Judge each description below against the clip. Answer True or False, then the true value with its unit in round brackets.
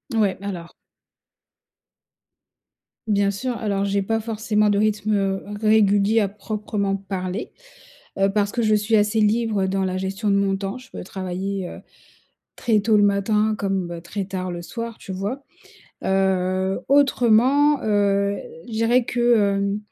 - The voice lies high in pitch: True (205 Hz)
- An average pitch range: False (2.1 semitones)